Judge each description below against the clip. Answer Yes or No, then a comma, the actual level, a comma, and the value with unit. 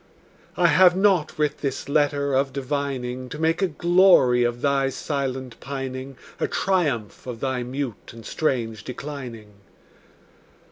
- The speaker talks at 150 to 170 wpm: No, slow, 135 wpm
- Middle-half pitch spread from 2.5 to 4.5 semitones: Yes, average, 3.1 semitones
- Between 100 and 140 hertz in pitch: Yes, low, 135 Hz